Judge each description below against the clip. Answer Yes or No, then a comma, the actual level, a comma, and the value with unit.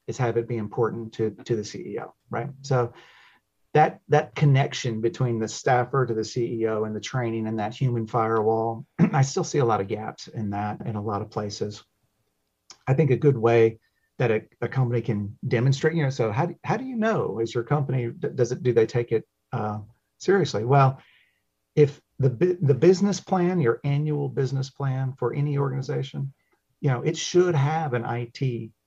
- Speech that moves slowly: No, average, 190 wpm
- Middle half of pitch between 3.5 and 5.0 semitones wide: Yes, average, 4.3 semitones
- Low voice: Yes, low, 125 Hz